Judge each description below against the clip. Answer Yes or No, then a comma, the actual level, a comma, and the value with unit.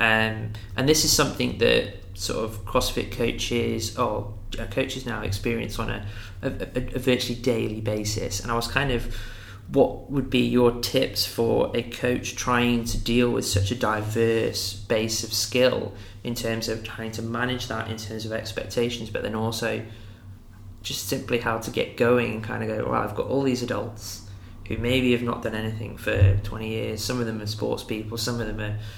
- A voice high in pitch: No, low, 110 Hz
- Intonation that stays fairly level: Yes, narrow, 2.3 semitones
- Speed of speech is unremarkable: Yes, average, 195 wpm